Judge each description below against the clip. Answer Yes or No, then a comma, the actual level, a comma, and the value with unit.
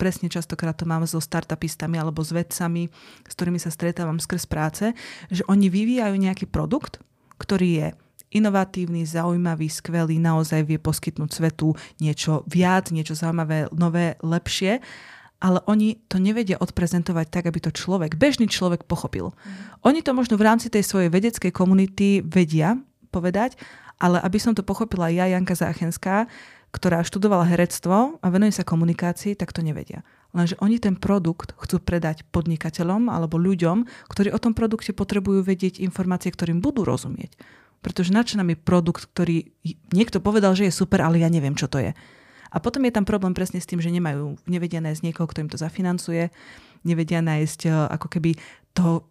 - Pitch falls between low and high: Yes, medium, 175 Hz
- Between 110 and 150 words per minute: No, fast, 165 wpm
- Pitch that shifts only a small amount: No, average, 3.1 semitones